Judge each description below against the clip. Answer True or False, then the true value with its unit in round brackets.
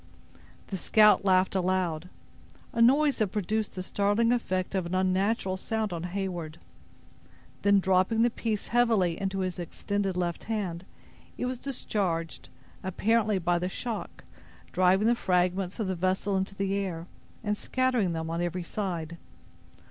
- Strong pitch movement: False (3.0 semitones)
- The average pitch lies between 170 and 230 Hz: True (190 Hz)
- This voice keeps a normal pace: True (145 wpm)